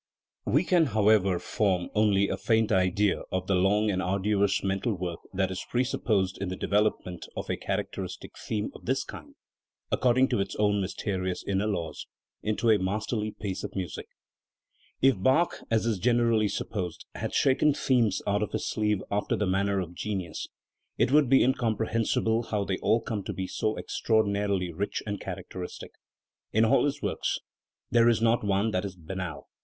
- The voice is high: No, low, 105 Hz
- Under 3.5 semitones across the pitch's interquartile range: Yes, average, 2.9 semitones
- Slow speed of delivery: No, average, 180 wpm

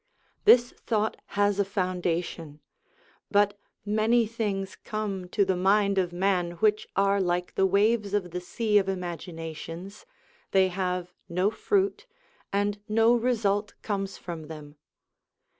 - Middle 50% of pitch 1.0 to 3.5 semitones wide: Yes, average, 2.9 semitones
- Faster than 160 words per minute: No, slow, 135 wpm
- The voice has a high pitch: Yes, high, 195 Hz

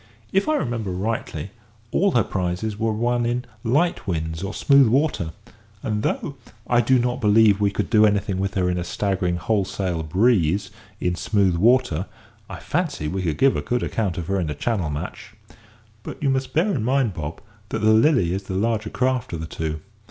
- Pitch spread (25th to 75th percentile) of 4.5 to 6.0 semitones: Yes, average, 5.3 semitones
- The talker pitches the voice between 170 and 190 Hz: No, low, 105 Hz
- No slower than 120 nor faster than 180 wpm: No, average, 200 wpm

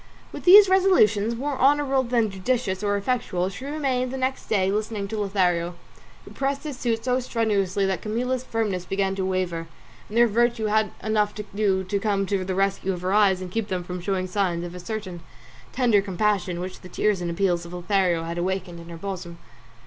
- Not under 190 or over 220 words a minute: Yes, average, 200 wpm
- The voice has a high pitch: Yes, high, 200 Hz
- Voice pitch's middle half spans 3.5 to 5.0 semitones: Yes, average, 3.9 semitones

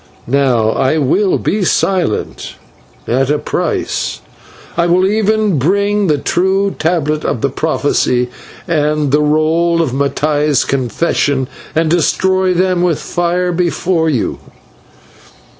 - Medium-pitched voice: Yes, medium, 160 Hz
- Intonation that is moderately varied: Yes, average, 4.3 semitones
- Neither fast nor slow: No, slow, 120 wpm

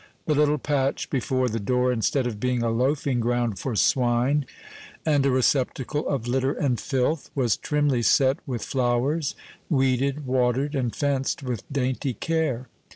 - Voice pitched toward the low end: Yes, low, 130 Hz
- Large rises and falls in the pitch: No, narrow, 2.6 semitones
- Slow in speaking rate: No, average, 155 wpm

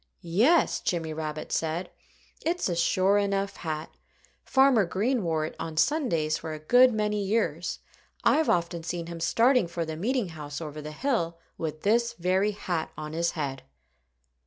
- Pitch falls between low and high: Yes, medium, 175 Hz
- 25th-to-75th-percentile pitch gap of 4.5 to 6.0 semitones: Yes, average, 5.3 semitones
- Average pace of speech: Yes, average, 160 wpm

